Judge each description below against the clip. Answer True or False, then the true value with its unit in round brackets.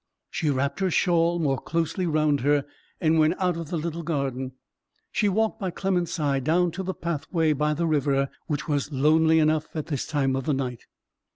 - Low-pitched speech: False (155 Hz)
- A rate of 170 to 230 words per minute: True (195 wpm)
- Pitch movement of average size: True (3.1 semitones)